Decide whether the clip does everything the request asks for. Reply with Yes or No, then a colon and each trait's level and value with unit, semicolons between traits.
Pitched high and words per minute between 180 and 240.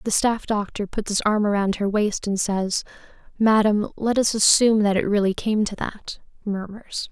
Yes: high, 210 Hz; average, 185 wpm